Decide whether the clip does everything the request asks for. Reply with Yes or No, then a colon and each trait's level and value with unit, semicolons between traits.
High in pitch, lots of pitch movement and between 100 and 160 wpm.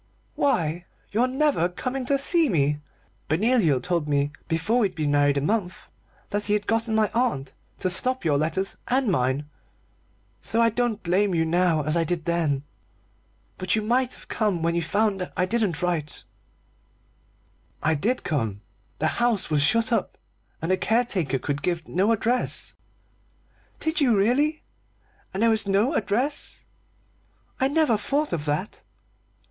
Yes: high, 195 Hz; wide, 6.6 semitones; average, 155 wpm